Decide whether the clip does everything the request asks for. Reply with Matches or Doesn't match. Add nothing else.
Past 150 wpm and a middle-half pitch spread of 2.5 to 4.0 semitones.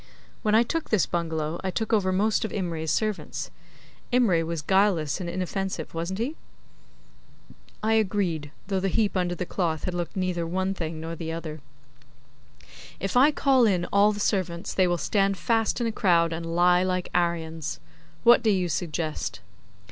Matches